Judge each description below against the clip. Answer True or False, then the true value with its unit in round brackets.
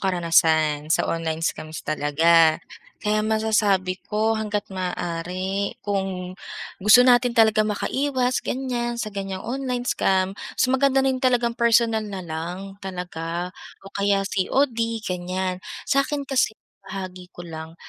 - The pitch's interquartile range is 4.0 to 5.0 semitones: True (4.7 semitones)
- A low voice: False (195 Hz)